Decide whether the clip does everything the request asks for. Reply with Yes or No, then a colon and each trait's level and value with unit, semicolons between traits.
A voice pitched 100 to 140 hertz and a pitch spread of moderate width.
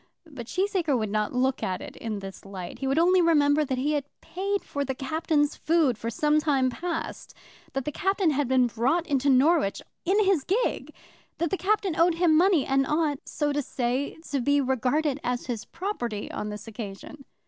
No: very high, 285 Hz; average, 4.8 semitones